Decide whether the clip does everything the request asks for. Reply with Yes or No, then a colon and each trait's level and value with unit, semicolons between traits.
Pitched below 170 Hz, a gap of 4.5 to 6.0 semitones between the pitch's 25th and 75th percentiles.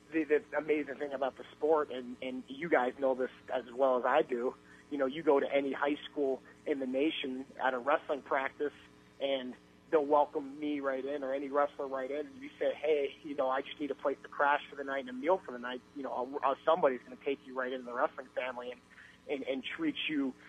No: low, 135 Hz; narrow, 2.6 semitones